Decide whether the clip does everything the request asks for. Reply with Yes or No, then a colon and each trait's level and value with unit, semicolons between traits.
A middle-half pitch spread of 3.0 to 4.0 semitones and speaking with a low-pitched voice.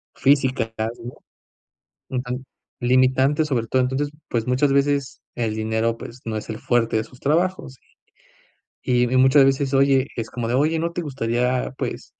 No: narrow, 2.6 semitones; low, 130 Hz